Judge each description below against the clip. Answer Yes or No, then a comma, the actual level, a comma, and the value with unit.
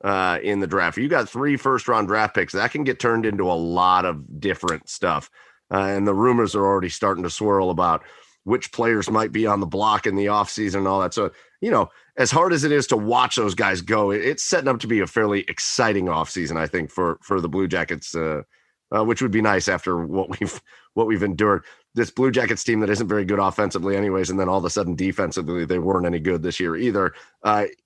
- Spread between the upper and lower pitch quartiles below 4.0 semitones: Yes, narrow, 2.6 semitones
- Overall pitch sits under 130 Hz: Yes, low, 100 Hz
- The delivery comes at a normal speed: No, fast, 235 wpm